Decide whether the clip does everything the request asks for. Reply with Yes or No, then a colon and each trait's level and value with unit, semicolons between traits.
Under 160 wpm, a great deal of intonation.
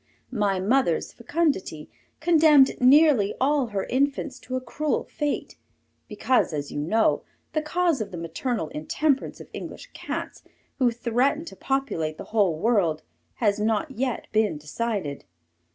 Yes: average, 140 wpm; wide, 6.2 semitones